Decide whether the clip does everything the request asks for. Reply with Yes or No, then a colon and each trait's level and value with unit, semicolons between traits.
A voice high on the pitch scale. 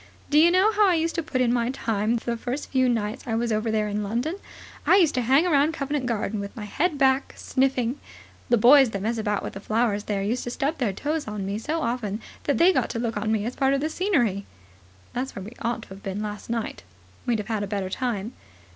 Yes: high, 235 Hz